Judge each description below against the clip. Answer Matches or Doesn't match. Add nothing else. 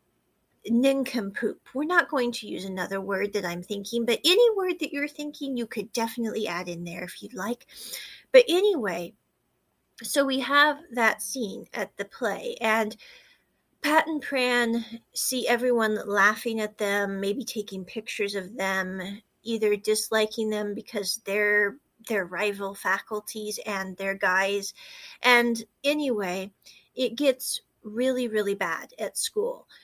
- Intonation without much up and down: Doesn't match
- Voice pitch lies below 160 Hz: Doesn't match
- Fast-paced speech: Doesn't match